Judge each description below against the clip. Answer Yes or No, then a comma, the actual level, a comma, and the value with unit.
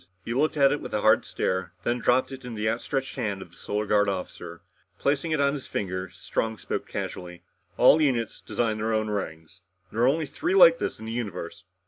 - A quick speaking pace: Yes, fast, 215 wpm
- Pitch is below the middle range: Yes, low, 110 Hz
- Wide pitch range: Yes, wide, 6.1 semitones